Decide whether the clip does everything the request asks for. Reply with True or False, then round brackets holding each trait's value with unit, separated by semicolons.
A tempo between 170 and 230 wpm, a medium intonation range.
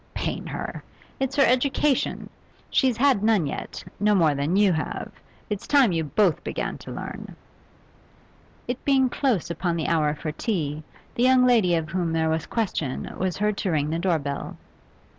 False (175 wpm; 7.2 semitones)